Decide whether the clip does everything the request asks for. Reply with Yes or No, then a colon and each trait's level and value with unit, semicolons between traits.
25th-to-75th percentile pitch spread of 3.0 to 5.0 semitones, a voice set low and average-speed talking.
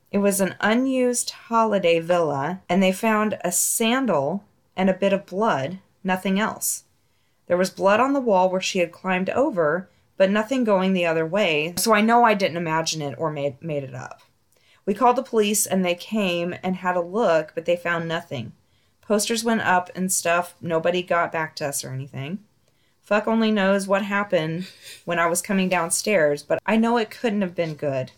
No: average, 3.7 semitones; medium, 185 Hz; average, 195 wpm